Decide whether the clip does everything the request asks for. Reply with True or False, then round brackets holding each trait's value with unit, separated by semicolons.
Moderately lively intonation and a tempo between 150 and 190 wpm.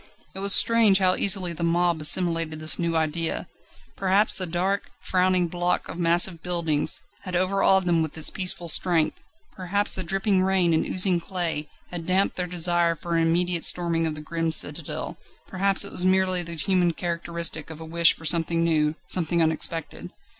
False (2.1 semitones; 175 wpm)